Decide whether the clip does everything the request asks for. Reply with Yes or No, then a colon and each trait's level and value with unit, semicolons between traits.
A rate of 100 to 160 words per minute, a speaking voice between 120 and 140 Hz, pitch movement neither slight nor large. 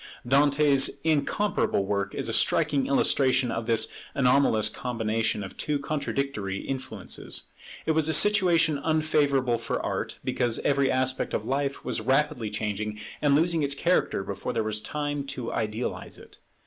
Yes: average, 150 wpm; low, 135 Hz; average, 4.8 semitones